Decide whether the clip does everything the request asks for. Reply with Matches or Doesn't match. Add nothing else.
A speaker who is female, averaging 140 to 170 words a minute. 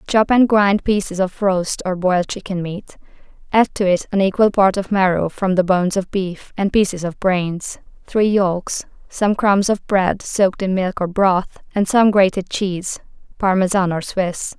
Doesn't match